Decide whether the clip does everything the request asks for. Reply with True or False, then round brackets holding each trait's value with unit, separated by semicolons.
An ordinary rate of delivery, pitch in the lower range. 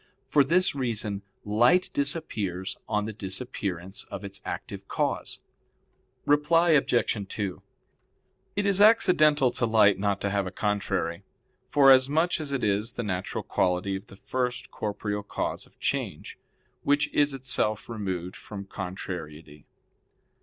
False (130 wpm; 105 Hz)